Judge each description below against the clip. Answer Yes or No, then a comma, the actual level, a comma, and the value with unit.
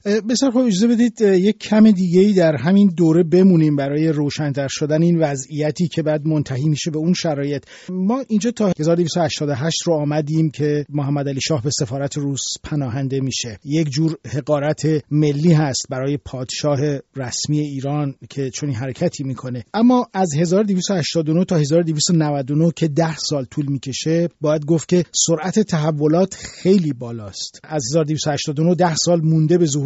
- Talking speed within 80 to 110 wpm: No, average, 150 wpm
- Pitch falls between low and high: Yes, medium, 155 Hz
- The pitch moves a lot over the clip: No, average, 3.3 semitones